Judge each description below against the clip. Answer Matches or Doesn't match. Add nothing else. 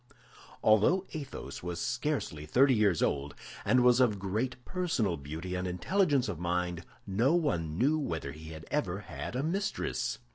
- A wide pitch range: Matches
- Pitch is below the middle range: Matches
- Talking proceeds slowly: Doesn't match